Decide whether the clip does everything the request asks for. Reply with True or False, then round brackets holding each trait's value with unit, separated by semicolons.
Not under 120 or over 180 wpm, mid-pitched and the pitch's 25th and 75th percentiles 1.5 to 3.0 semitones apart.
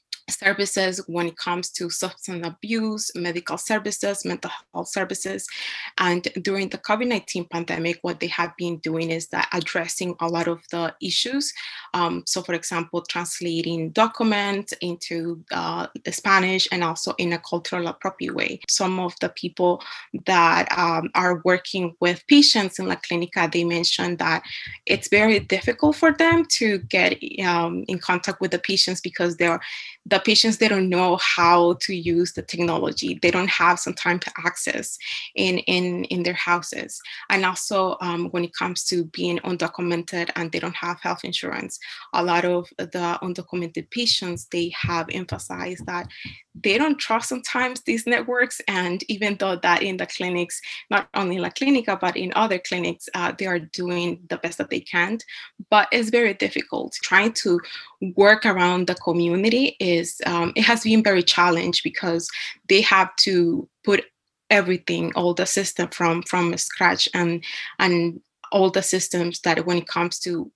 True (165 wpm; 180 Hz; 2.4 semitones)